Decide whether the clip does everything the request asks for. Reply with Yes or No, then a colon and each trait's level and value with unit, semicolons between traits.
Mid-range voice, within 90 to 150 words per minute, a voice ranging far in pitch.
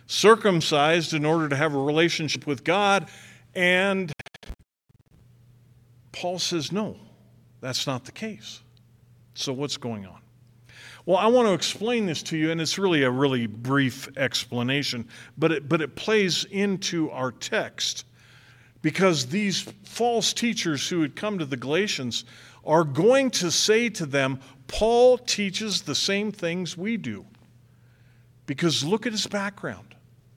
Yes: medium, 150 Hz; average, 140 wpm; wide, 7.5 semitones